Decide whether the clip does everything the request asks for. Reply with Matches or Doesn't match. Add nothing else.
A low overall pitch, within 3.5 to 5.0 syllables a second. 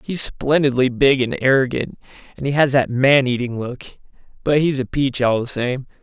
Matches